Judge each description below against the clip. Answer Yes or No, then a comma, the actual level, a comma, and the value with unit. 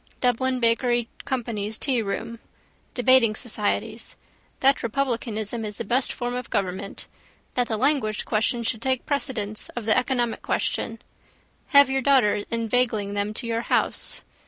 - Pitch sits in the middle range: No, high, 235 Hz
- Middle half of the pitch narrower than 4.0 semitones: Yes, average, 2.9 semitones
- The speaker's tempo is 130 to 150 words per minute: Yes, slow, 135 wpm